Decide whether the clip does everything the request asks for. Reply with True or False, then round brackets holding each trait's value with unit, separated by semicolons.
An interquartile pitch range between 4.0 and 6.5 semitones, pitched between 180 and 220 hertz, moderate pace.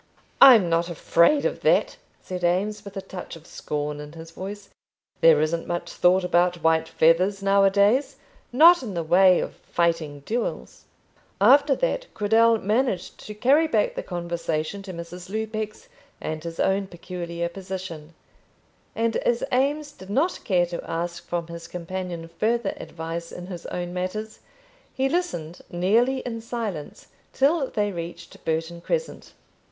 True (4.8 semitones; 185 Hz; 155 wpm)